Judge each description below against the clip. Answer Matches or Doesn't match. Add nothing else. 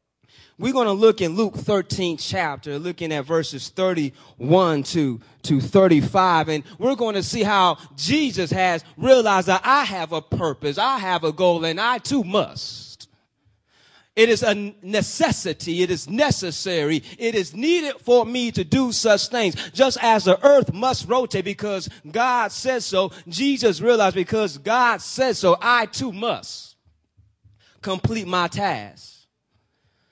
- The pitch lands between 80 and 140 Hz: Doesn't match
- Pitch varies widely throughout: Matches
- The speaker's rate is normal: Matches